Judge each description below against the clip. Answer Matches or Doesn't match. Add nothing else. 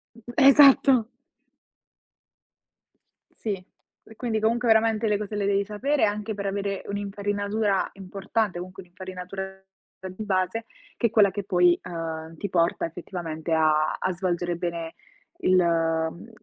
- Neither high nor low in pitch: Doesn't match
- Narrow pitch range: Doesn't match